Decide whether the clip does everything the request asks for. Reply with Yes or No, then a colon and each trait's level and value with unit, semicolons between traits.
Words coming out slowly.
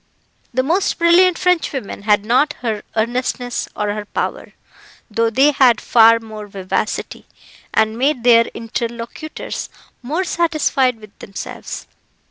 Yes: slow, 120 wpm